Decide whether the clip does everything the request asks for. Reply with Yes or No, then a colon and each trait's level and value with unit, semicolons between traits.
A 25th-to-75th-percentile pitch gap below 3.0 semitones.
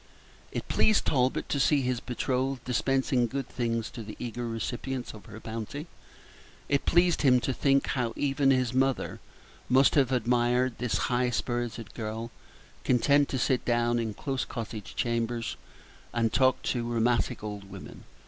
Yes: narrow, 2.4 semitones